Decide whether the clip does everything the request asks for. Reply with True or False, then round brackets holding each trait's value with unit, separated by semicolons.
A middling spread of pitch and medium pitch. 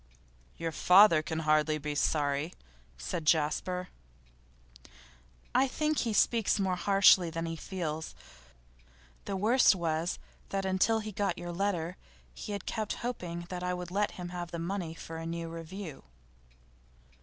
True (3.3 semitones; 175 Hz)